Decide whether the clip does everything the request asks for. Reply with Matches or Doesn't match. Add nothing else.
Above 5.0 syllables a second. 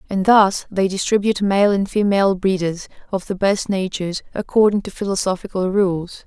Matches